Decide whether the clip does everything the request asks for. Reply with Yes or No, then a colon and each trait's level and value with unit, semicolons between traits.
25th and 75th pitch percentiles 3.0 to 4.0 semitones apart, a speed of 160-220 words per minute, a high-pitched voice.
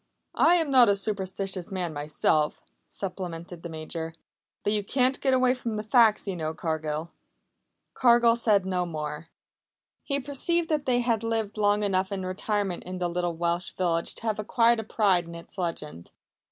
No: average, 5.1 semitones; average, 175 wpm; high, 195 Hz